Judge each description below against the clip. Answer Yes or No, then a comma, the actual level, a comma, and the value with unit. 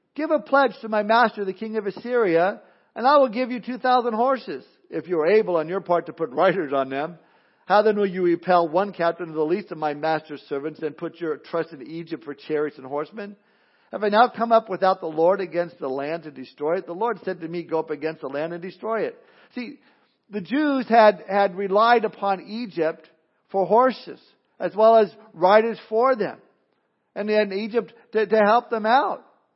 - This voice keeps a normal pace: No, fast, 215 wpm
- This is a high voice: Yes, high, 195 Hz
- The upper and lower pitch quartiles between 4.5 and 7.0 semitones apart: Yes, wide, 5.4 semitones